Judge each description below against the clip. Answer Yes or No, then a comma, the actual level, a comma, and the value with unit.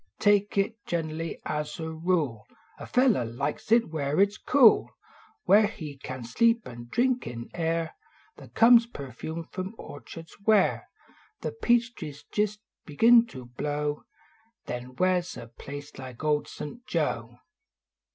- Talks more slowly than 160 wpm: Yes, average, 150 wpm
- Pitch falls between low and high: Yes, medium, 165 Hz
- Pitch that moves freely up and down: Yes, wide, 7.1 semitones